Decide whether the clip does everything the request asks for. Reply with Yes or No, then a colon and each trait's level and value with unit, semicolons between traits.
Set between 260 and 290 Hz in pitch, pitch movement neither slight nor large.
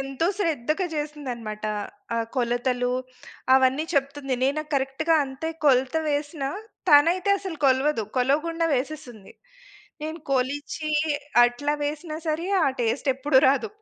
Yes: very high, 280 Hz; average, 3.1 semitones